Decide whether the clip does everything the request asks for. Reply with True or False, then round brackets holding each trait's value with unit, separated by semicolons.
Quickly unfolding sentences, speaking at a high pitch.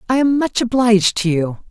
True (210 wpm; 220 Hz)